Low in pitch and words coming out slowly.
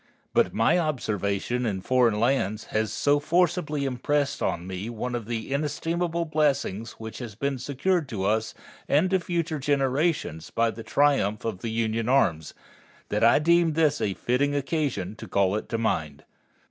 No: low, 125 Hz; average, 165 wpm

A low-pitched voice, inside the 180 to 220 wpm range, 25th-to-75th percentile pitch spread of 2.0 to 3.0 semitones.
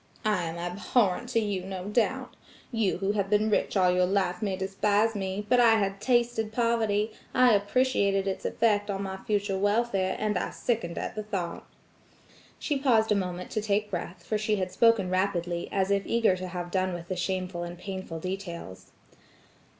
No: high, 200 Hz; average, 185 wpm; average, 2.7 semitones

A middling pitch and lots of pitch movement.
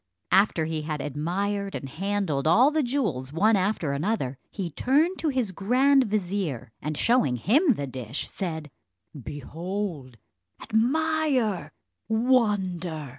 No: high, 195 Hz; wide, 7.5 semitones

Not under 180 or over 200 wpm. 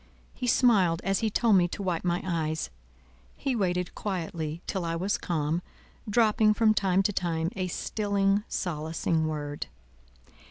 No: average, 150 wpm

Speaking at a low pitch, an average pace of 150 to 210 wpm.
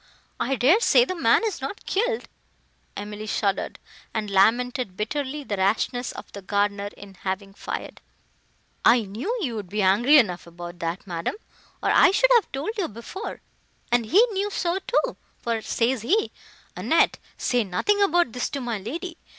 No: high, 240 Hz; average, 165 wpm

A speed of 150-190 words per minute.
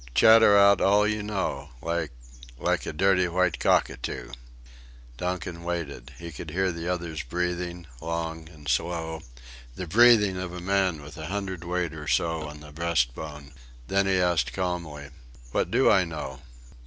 Yes: average, 155 wpm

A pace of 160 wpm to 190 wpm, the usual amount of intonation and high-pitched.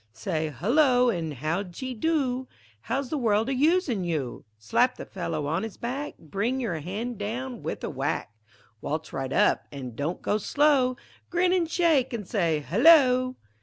No: average, 165 wpm; wide, 7.9 semitones; high, 230 Hz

